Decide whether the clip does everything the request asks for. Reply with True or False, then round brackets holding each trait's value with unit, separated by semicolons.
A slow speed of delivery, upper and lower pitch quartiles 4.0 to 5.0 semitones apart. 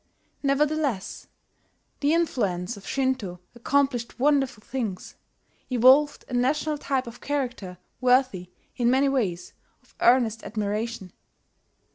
True (105 wpm; 4.4 semitones)